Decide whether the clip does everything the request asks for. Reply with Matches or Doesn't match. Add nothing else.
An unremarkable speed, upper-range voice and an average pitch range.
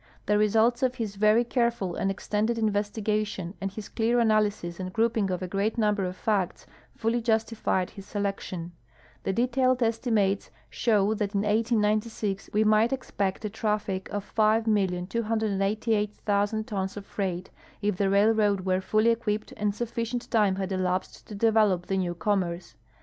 Doesn't match